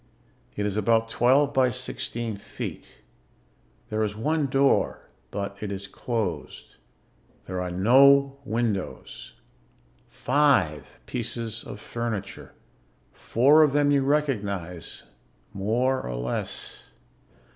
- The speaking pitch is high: No, low, 115 Hz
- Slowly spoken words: Yes, slow, 105 wpm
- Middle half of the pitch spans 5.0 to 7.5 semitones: Yes, average, 5.3 semitones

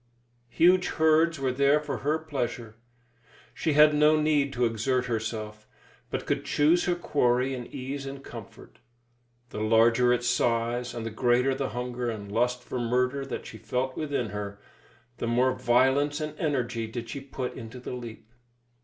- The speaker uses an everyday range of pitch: Yes, average, 3.3 semitones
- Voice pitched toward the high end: No, low, 125 Hz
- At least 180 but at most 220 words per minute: No, average, 165 wpm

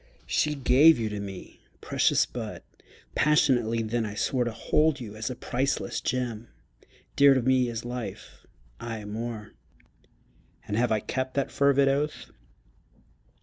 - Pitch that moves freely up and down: No, average, 3.5 semitones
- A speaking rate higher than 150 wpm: No, average, 145 wpm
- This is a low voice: Yes, low, 125 Hz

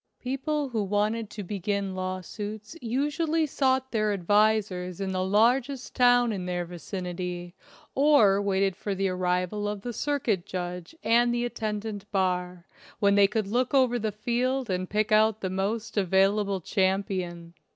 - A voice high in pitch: Yes, high, 205 Hz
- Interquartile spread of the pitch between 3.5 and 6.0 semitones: Yes, average, 4.1 semitones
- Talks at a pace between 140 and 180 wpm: Yes, average, 150 wpm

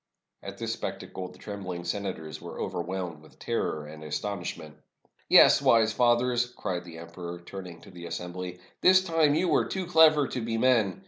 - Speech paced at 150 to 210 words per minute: Yes, average, 175 wpm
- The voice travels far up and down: Yes, wide, 6.0 semitones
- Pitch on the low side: Yes, very low, 95 Hz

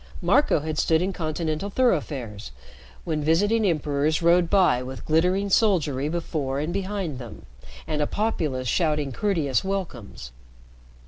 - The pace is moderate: No, slow, 130 wpm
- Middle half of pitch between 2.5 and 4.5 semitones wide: No, average, 4.9 semitones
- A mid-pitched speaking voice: Yes, medium, 160 Hz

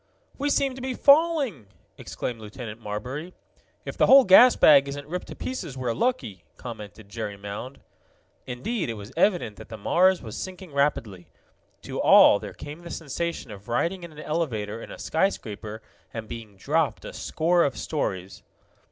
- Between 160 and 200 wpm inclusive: Yes, average, 170 wpm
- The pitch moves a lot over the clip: Yes, wide, 8.4 semitones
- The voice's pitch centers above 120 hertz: Yes, medium, 140 Hz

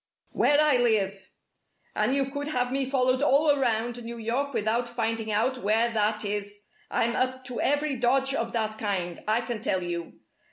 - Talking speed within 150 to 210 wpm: Yes, average, 175 wpm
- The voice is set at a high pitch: Yes, high, 235 Hz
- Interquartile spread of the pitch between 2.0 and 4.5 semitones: Yes, average, 3.4 semitones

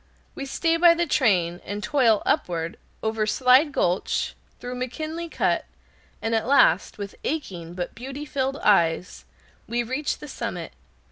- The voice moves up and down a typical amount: No, wide, 6.3 semitones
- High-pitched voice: Yes, high, 245 Hz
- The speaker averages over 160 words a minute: No, average, 145 wpm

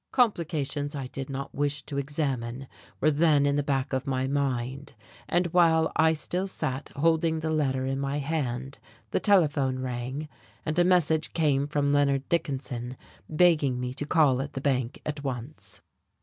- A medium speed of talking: Yes, average, 165 wpm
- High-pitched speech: No, medium, 145 Hz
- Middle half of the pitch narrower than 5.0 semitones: Yes, average, 2.9 semitones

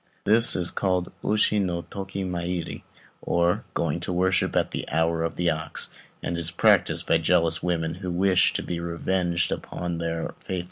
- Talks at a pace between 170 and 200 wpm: Yes, average, 180 wpm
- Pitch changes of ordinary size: No, narrow, 1.7 semitones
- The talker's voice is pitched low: Yes, very low, 85 Hz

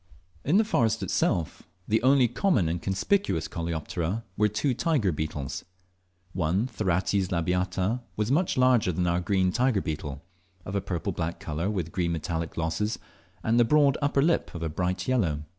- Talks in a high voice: No, very low, 95 Hz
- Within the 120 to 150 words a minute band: No, average, 165 wpm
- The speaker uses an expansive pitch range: Yes, wide, 6.3 semitones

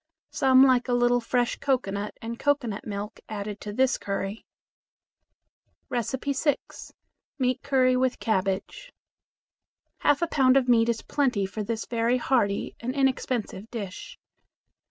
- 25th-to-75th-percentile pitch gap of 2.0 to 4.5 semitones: Yes, average, 3.8 semitones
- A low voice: No, high, 245 Hz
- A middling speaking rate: No, slow, 130 wpm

